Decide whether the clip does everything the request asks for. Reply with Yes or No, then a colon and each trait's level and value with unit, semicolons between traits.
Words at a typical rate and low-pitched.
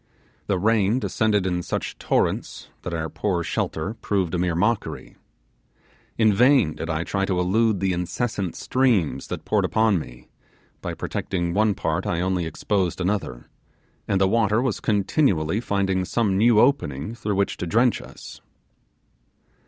Yes: average, 150 wpm; very low, 95 Hz